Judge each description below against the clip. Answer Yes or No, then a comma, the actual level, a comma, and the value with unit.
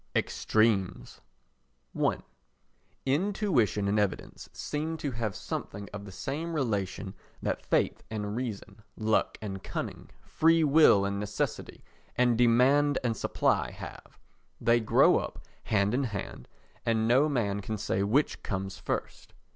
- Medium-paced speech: No, slow, 130 wpm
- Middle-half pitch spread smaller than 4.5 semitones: No, average, 5.2 semitones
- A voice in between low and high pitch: No, low, 110 Hz